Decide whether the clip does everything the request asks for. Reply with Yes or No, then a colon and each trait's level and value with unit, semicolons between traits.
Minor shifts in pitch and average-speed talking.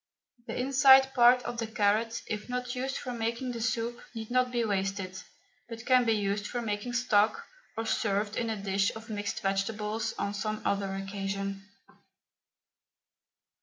No: average, 3.1 semitones; average, 160 wpm